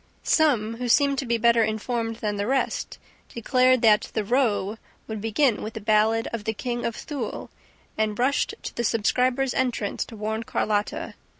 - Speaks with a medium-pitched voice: No, high, 230 Hz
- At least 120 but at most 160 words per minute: No, average, 175 wpm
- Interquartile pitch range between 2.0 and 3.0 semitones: Yes, narrow, 2.6 semitones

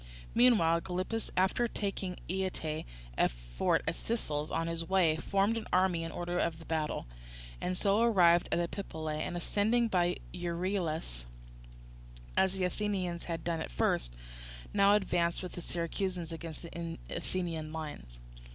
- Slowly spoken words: No, average, 145 wpm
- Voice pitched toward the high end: No, medium, 175 Hz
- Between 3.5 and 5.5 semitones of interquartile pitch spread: No, average, 2.8 semitones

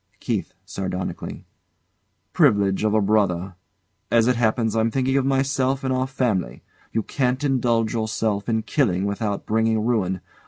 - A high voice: No, low, 110 Hz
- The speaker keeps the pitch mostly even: No, average, 4.0 semitones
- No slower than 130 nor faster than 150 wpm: Yes, average, 145 wpm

